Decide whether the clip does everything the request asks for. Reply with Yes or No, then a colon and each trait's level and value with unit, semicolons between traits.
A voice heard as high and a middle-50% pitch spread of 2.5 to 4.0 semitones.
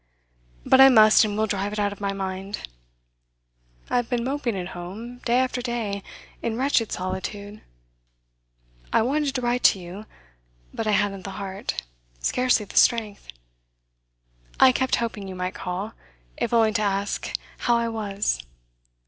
Yes: high, 215 Hz; average, 3.4 semitones